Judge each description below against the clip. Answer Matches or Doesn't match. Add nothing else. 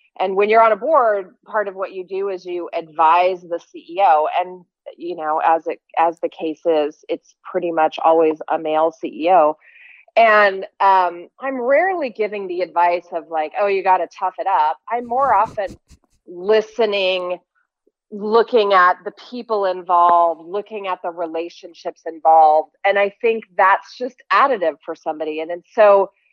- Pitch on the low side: Doesn't match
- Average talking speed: Matches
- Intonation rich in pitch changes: Doesn't match